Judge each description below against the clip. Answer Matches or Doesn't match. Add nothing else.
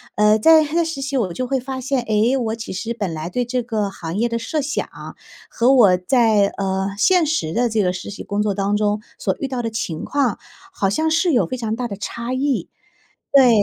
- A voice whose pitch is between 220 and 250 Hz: Matches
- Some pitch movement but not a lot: Matches